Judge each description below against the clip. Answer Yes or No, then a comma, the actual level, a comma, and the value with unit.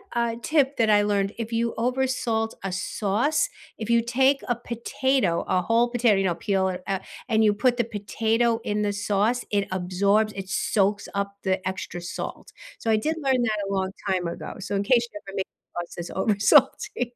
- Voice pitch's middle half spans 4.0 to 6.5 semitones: No, average, 3.5 semitones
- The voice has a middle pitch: No, high, 215 Hz